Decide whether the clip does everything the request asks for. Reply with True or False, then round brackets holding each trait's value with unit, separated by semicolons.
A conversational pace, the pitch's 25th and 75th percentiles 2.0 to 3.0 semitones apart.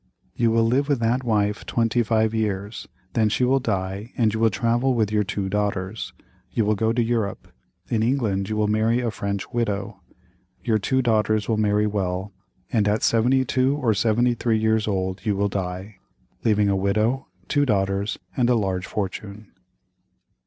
True (175 wpm; 2.6 semitones)